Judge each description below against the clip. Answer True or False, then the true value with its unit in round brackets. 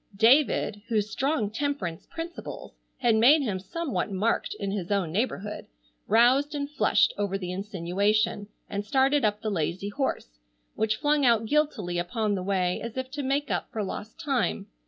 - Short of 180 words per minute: True (165 wpm)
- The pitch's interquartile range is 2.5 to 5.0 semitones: False (5.4 semitones)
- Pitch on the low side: False (215 Hz)